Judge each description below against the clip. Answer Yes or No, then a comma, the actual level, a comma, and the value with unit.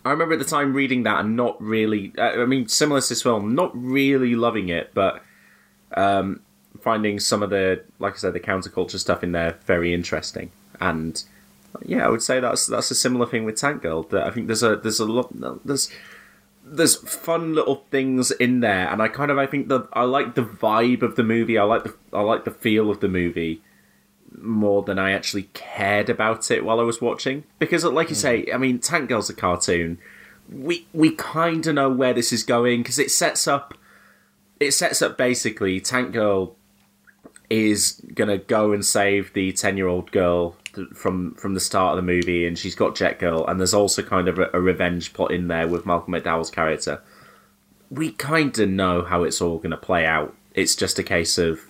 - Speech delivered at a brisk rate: Yes, fast, 210 wpm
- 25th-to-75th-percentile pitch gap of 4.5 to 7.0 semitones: Yes, average, 5.3 semitones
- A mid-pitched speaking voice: No, low, 105 Hz